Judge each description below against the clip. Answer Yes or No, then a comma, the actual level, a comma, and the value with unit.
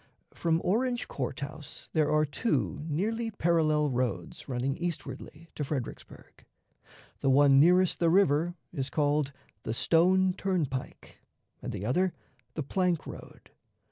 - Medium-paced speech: No, slow, 130 wpm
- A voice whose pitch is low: No, medium, 155 Hz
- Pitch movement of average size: Yes, average, 4.5 semitones